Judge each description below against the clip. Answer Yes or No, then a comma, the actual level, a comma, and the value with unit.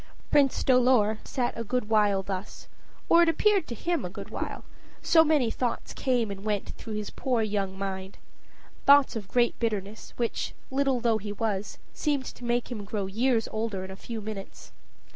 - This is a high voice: Yes, high, 225 Hz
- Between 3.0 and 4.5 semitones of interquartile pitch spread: Yes, average, 3.9 semitones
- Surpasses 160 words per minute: Yes, average, 180 wpm